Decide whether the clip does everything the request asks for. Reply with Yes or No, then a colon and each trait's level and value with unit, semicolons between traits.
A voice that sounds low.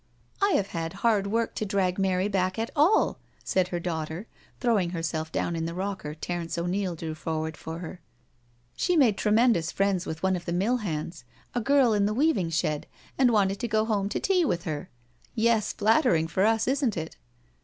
No: high, 190 Hz